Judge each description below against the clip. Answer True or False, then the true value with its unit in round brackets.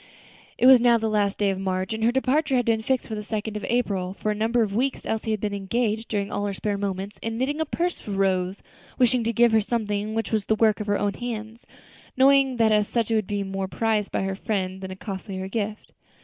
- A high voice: True (215 Hz)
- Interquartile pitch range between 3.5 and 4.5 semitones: False (2.7 semitones)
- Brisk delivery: True (250 wpm)